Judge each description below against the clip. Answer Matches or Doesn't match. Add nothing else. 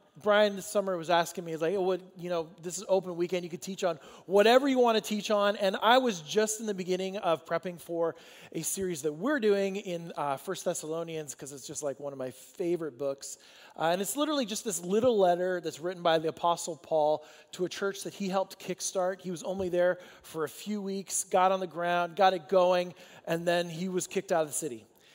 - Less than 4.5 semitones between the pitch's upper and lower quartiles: Matches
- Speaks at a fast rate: Matches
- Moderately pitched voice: Matches